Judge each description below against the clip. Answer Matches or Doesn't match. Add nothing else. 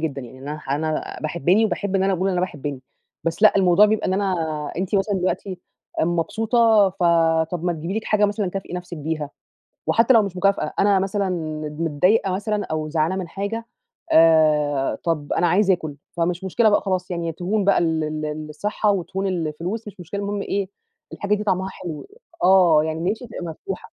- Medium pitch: Matches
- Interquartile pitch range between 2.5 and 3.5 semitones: Doesn't match